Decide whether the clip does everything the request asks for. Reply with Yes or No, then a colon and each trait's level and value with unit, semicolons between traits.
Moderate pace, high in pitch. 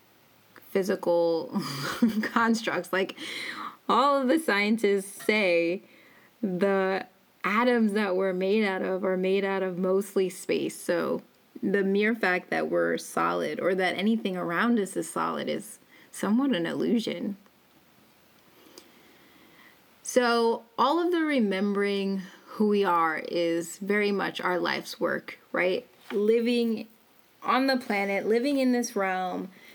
No: slow, 125 wpm; high, 200 Hz